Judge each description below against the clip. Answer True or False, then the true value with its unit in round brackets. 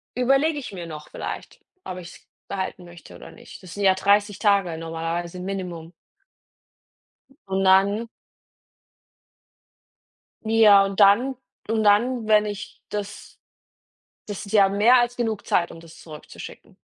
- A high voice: True (200 Hz)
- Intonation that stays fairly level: False (3.3 semitones)